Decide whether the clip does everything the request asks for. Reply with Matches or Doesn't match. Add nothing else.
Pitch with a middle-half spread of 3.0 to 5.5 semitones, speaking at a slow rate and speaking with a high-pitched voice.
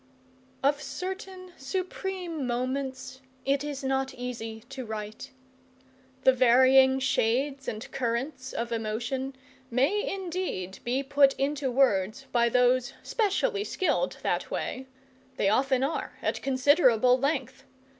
Doesn't match